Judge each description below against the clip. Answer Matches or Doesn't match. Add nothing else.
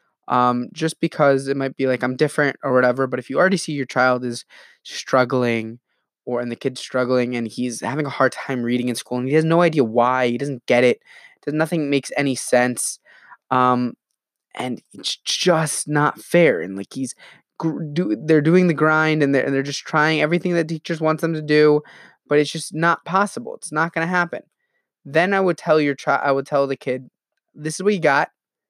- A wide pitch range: Doesn't match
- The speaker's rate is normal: Doesn't match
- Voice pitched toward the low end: Doesn't match